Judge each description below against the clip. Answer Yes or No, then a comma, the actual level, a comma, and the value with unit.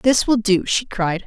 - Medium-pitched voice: No, high, 210 Hz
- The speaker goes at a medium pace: No, fast, 240 wpm